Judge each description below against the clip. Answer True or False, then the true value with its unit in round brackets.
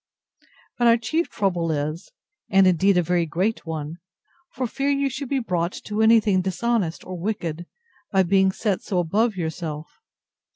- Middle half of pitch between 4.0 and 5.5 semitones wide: True (4.9 semitones)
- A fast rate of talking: False (160 wpm)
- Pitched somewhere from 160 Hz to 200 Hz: True (190 Hz)